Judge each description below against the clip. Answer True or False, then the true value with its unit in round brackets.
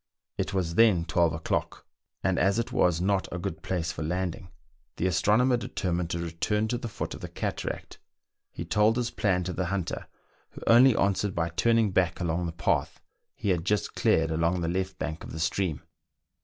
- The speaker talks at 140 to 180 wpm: False (195 wpm)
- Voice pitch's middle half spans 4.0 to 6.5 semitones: False (3.4 semitones)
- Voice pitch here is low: True (90 Hz)